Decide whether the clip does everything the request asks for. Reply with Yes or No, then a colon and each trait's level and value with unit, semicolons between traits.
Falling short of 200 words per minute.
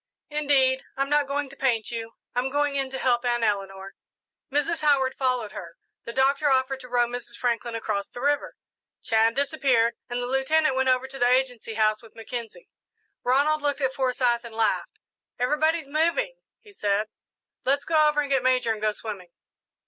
Yes: average, 180 wpm